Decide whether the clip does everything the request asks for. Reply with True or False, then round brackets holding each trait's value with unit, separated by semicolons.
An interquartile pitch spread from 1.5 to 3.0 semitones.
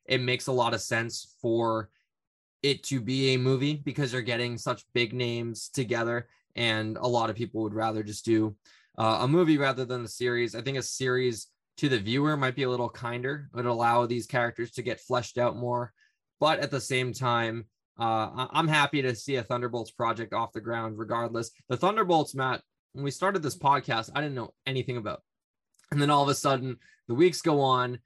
True (2.7 semitones)